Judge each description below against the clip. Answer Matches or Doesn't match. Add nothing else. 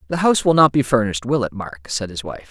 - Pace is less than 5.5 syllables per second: Doesn't match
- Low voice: Matches